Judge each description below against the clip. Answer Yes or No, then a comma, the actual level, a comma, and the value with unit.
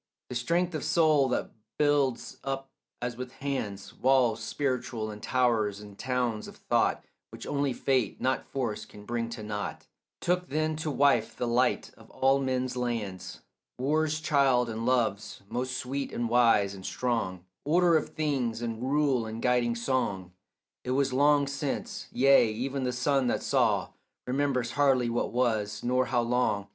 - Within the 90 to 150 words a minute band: No, average, 160 wpm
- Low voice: Yes, low, 125 Hz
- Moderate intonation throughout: Yes, average, 3.0 semitones